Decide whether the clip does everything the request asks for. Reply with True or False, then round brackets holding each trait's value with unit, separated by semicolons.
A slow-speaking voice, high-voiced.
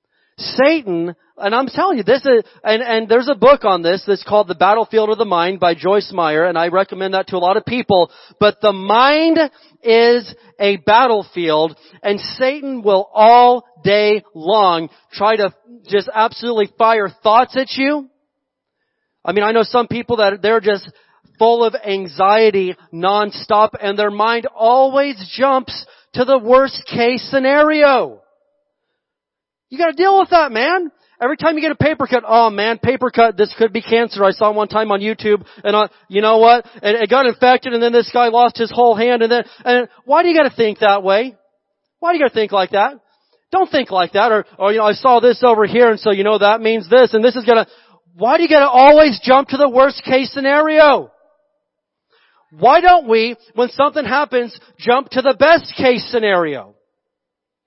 False (195 wpm; 230 Hz)